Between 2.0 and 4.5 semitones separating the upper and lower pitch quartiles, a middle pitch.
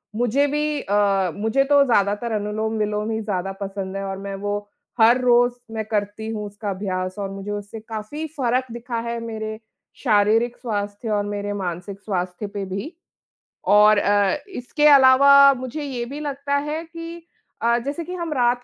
No: average, 3.8 semitones; high, 220 Hz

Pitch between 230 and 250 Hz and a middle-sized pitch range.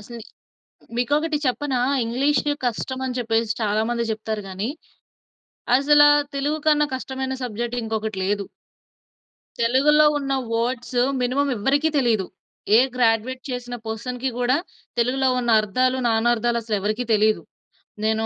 Yes: high, 245 Hz; average, 3.0 semitones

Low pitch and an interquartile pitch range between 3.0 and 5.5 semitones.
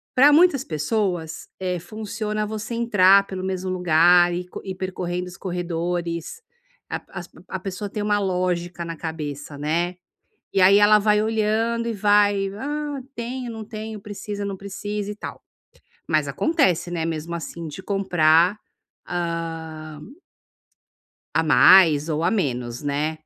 No: medium, 185 Hz; average, 4.0 semitones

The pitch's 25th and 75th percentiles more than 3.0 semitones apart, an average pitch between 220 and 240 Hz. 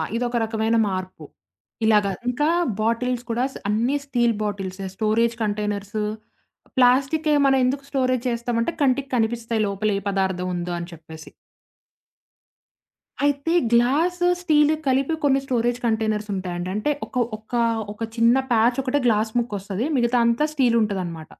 Yes: average, 3.6 semitones; high, 230 Hz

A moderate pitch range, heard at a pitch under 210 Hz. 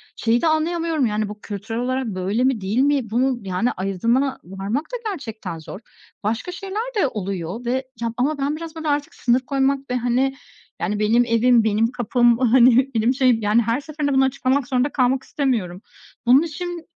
No: average, 3.9 semitones; very high, 250 Hz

